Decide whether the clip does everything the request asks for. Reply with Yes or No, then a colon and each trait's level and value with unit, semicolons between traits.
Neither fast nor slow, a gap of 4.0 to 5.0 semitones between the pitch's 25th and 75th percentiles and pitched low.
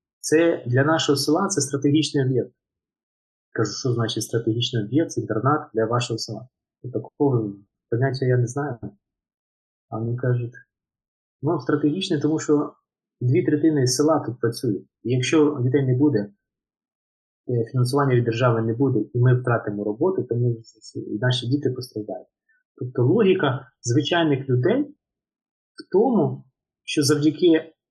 Yes: average, 130 wpm; average, 4.7 semitones; low, 125 Hz